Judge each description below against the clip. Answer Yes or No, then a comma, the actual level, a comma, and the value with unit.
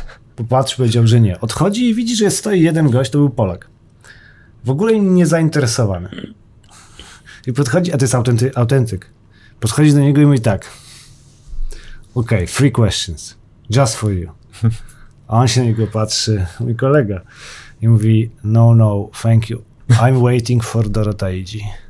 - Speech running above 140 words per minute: Yes, average, 150 wpm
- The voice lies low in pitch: Yes, low, 120 Hz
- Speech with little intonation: No, average, 3.6 semitones